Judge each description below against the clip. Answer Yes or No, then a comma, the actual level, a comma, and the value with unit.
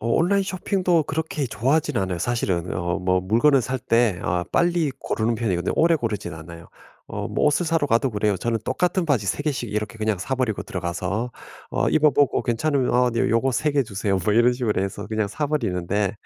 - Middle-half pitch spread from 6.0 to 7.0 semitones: Yes, wide, 6.4 semitones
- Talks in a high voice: No, low, 115 Hz